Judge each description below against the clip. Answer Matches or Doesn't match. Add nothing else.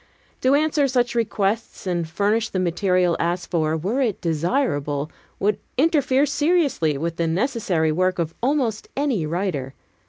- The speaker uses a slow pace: Doesn't match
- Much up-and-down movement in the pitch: Matches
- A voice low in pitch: Doesn't match